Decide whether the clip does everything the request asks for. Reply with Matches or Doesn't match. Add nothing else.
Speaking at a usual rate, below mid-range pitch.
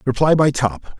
Matches